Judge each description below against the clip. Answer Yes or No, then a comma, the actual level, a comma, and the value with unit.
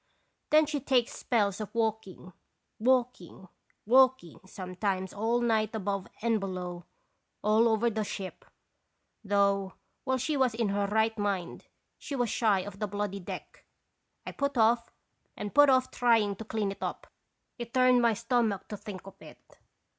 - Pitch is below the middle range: No, high, 220 Hz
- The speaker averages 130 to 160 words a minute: Yes, average, 155 wpm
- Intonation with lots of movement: No, average, 3.2 semitones